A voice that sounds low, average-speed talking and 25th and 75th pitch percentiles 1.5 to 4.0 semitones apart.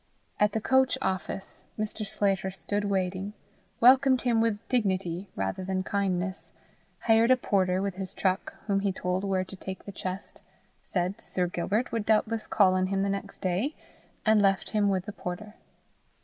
No: high, 195 Hz; average, 170 wpm; narrow, 2.5 semitones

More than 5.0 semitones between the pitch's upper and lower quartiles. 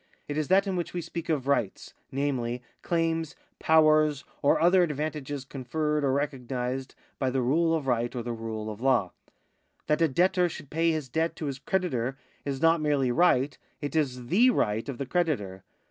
No: average, 4.3 semitones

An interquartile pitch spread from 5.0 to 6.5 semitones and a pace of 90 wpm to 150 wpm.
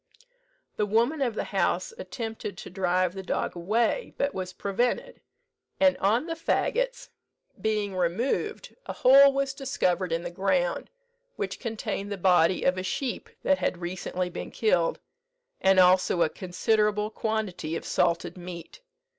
Yes: wide, 5.4 semitones; average, 145 wpm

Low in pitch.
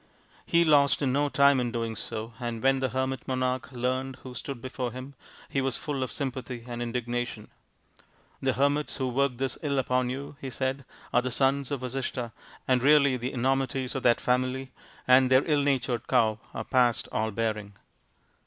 Yes: low, 130 Hz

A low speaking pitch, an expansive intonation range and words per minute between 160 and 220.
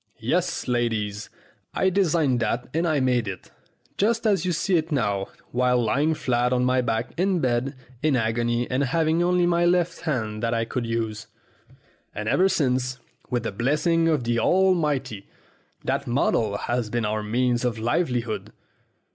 Yes: low, 125 Hz; wide, 5.9 semitones; average, 165 wpm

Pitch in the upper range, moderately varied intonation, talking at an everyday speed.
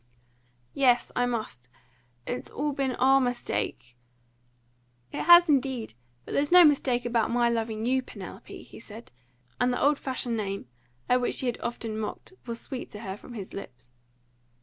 Yes: high, 240 Hz; average, 3.5 semitones; average, 170 wpm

